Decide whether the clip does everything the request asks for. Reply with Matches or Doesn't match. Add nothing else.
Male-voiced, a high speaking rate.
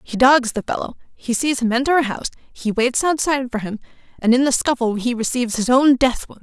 Doesn't match